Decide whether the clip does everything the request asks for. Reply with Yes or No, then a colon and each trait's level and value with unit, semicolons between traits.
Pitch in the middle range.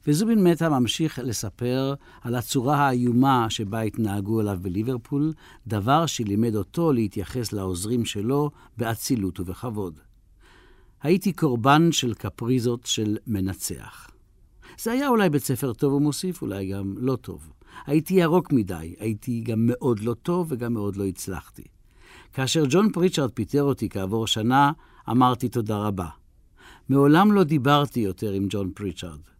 No: low, 120 Hz